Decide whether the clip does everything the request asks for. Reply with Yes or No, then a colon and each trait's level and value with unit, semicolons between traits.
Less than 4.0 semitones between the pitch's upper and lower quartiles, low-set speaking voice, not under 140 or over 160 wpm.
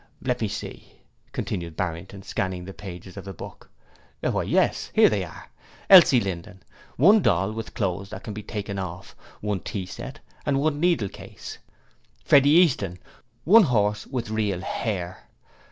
No: wide, 5.5 semitones; low, 100 Hz; average, 150 wpm